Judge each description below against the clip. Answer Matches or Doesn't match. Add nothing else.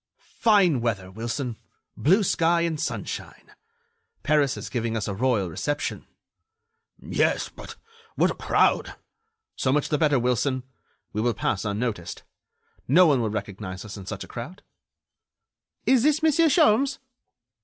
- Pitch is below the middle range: Matches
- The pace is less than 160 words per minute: Matches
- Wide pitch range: Matches